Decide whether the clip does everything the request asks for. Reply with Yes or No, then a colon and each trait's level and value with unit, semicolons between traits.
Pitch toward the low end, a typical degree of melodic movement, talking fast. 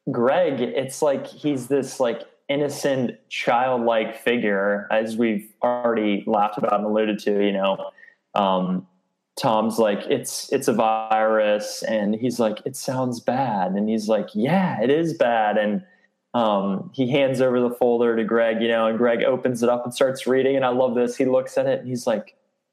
No: low, 115 Hz; average, 3.4 semitones; average, 180 wpm